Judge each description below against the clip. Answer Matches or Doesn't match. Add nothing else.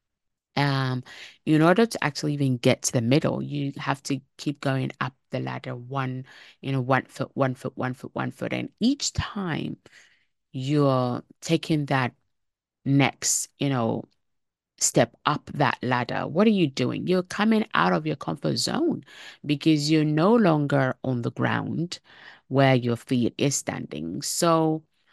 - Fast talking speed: Doesn't match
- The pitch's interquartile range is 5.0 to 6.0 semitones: Doesn't match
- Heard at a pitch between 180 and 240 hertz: Doesn't match